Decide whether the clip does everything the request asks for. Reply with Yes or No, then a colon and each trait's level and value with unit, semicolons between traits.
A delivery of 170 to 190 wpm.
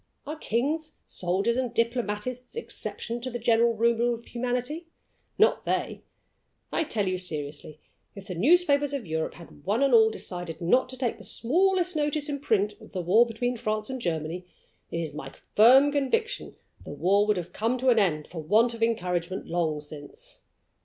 Yes: average, 180 wpm